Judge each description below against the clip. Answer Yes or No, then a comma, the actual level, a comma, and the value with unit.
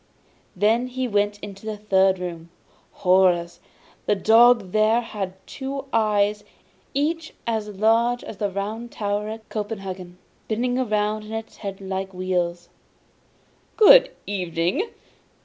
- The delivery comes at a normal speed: No, slow, 125 wpm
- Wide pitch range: No, average, 3.1 semitones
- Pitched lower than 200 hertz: No, high, 210 Hz